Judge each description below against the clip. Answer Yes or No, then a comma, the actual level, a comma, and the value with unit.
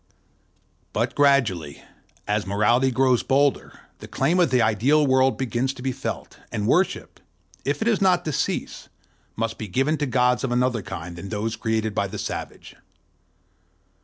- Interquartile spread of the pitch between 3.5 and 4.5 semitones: Yes, average, 4.0 semitones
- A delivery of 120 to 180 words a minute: Yes, average, 165 wpm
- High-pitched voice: No, low, 125 Hz